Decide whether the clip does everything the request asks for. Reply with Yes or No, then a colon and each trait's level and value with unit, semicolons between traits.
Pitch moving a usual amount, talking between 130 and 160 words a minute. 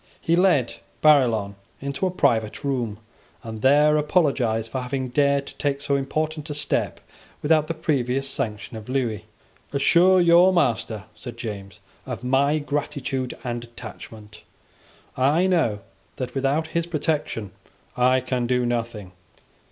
Yes: average, 4.3 semitones; slow, 135 wpm